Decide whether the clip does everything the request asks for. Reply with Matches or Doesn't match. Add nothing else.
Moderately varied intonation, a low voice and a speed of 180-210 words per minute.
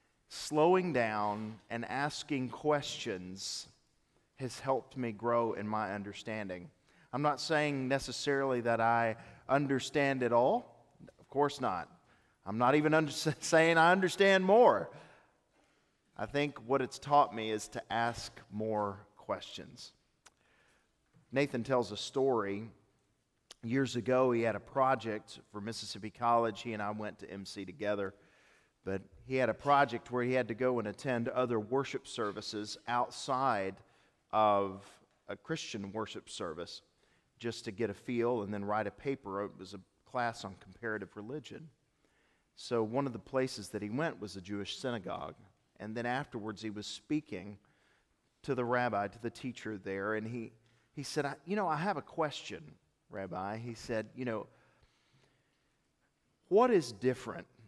Doesn't match